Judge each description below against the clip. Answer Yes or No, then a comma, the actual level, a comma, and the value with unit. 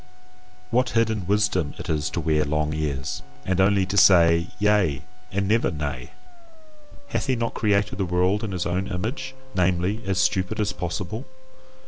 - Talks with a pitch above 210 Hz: No, very low, 95 Hz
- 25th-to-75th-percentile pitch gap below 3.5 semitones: No, average, 4.0 semitones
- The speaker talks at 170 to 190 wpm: No, average, 160 wpm